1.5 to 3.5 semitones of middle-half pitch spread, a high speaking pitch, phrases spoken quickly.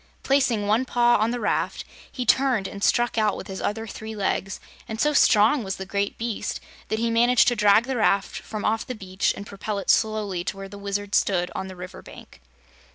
Yes: average, 2.9 semitones; high, 215 Hz; fast, 220 wpm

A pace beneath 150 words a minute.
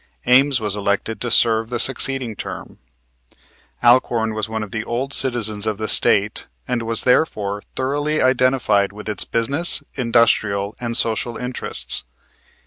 Yes: average, 140 wpm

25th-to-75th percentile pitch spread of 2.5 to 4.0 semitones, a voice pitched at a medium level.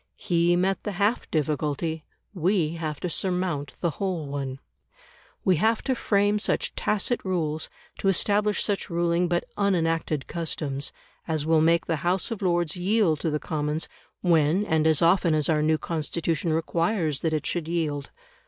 Yes: average, 3.3 semitones; medium, 170 Hz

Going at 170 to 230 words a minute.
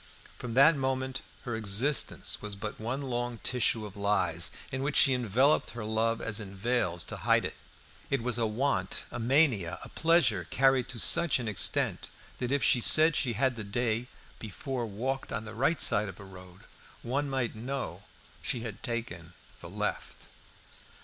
Yes: average, 175 wpm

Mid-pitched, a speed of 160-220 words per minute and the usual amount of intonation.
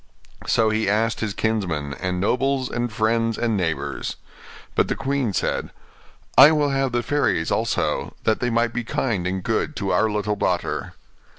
No: low, 110 Hz; average, 170 wpm; average, 3.4 semitones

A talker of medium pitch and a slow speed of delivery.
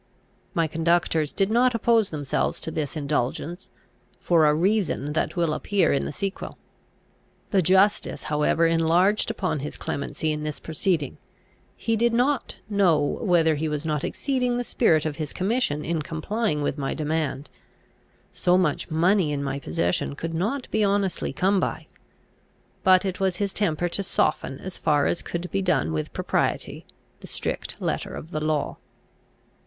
No: medium, 165 Hz; average, 160 wpm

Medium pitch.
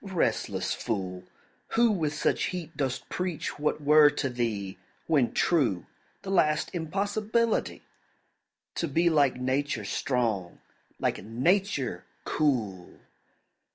Yes: medium, 145 Hz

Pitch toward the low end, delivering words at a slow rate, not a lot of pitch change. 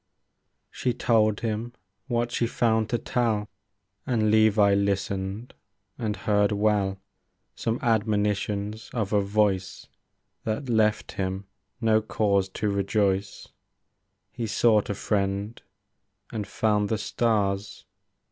Yes: low, 105 Hz; slow, 115 wpm; narrow, 2.0 semitones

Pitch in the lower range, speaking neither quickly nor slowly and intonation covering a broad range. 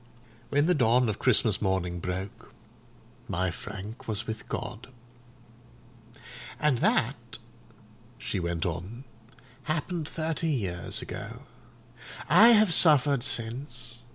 No: low, 120 Hz; slow, 105 wpm; wide, 6.6 semitones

